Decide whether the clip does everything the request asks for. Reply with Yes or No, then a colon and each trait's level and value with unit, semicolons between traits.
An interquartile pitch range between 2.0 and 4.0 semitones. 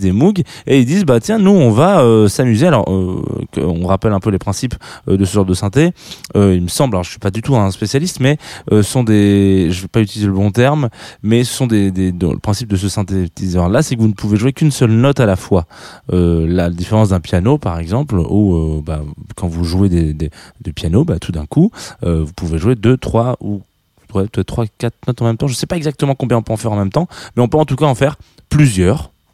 No: wide, 5.6 semitones